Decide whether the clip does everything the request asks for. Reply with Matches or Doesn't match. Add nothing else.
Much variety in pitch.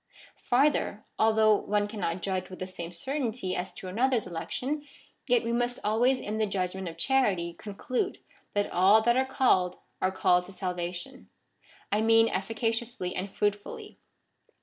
Doesn't match